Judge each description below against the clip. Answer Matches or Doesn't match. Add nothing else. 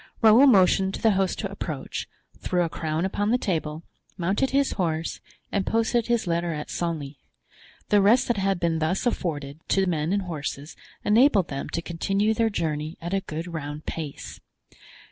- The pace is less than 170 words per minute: Doesn't match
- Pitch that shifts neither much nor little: Matches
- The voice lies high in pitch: Doesn't match